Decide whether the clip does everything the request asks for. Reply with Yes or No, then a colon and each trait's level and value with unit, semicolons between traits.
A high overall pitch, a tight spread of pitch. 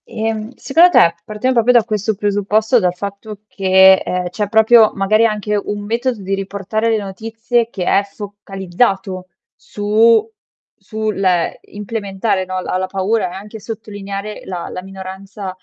Yes: high, 205 Hz; narrow, 2.3 semitones